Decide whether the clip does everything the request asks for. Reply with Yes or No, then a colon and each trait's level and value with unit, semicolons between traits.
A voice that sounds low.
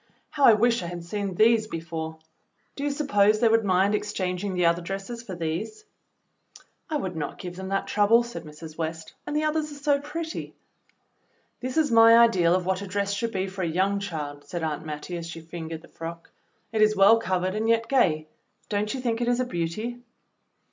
No: high, 200 Hz